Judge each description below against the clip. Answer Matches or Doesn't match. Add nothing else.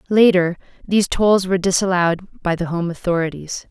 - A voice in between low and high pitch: Matches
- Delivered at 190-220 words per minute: Doesn't match